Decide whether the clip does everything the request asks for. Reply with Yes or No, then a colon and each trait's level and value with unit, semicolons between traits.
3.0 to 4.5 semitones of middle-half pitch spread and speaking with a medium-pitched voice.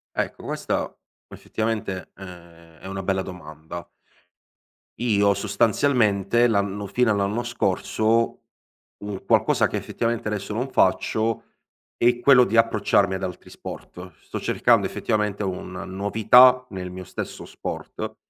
No: average, 3.4 semitones; low, 100 Hz